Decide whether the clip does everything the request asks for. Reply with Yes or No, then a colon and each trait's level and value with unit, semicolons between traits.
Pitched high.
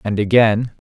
No: low, 110 Hz